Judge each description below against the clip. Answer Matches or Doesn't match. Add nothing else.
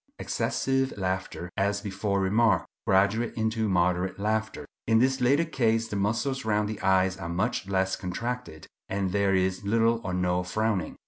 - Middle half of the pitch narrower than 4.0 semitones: Matches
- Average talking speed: Matches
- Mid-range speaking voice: Doesn't match